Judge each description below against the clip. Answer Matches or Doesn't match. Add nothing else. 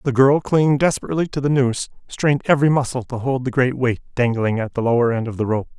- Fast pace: Matches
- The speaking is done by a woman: Doesn't match